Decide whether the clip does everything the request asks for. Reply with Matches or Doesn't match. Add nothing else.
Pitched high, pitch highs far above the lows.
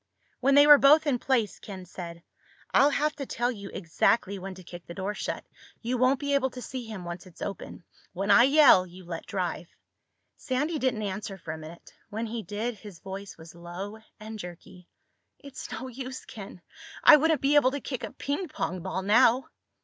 Matches